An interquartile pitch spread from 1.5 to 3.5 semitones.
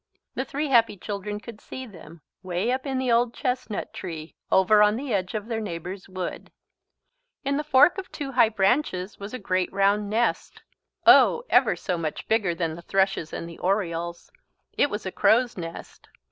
No: average, 5.0 semitones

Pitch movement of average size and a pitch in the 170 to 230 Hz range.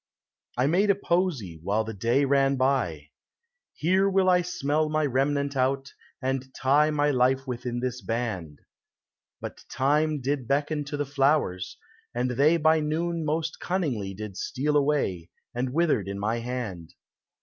No: average, 4.3 semitones; low, 135 Hz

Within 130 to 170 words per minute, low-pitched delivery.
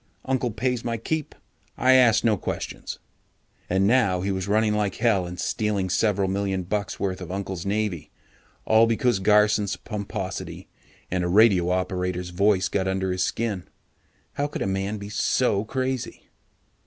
Yes: average, 155 wpm; low, 100 Hz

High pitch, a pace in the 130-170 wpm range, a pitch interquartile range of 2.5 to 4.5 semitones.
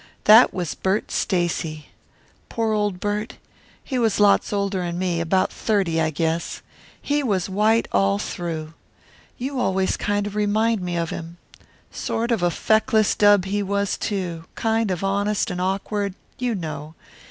Yes: high, 195 Hz; average, 155 wpm; average, 3.5 semitones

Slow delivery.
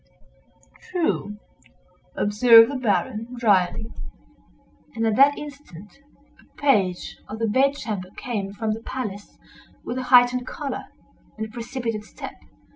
Yes: slow, 120 wpm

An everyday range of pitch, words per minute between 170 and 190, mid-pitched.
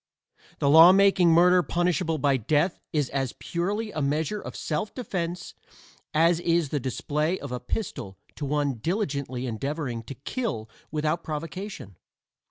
No: average, 4.3 semitones; average, 145 wpm; medium, 155 Hz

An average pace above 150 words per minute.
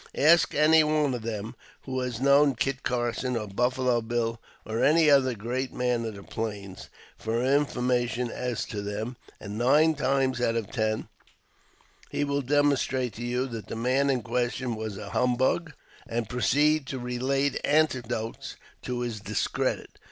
Yes: average, 160 wpm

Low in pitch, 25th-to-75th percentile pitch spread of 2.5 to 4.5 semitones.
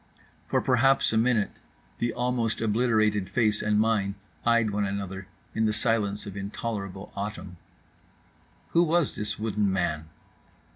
Yes: low, 105 Hz; average, 2.8 semitones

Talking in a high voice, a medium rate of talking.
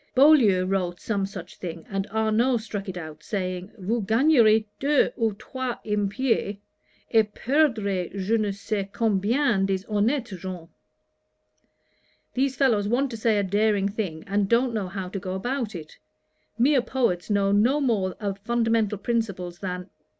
Yes: high, 210 Hz; average, 150 wpm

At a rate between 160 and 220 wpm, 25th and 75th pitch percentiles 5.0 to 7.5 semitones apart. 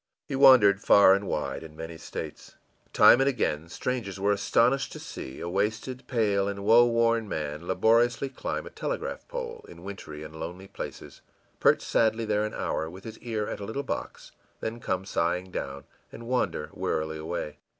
Yes: average, 180 wpm; wide, 5.5 semitones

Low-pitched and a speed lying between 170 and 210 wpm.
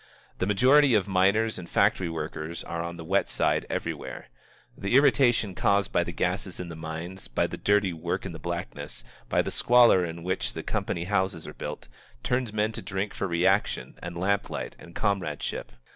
Yes: very low, 95 Hz; average, 185 wpm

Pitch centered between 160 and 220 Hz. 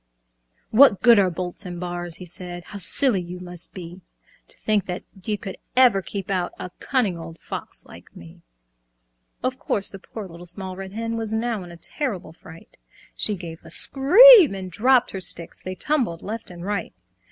Yes: high, 190 Hz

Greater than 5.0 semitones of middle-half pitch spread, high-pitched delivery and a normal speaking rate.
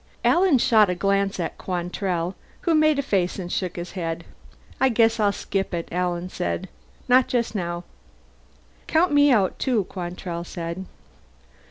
Yes: wide, 5.5 semitones; high, 195 Hz; average, 155 wpm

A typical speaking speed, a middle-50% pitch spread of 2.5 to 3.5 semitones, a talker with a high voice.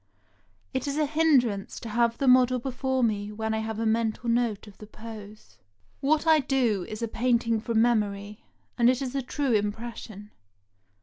Yes: average, 180 wpm; average, 3.1 semitones; high, 230 Hz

